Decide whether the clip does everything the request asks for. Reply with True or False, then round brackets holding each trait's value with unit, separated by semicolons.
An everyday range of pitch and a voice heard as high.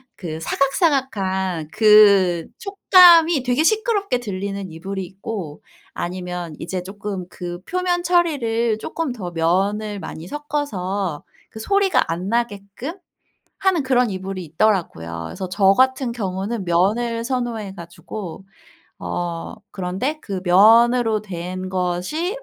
False (5.8 semitones; 200 Hz)